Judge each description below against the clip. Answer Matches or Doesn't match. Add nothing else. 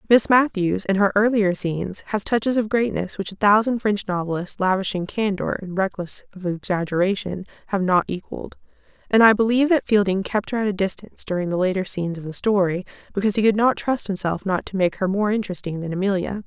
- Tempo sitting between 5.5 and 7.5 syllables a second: Matches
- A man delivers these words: Doesn't match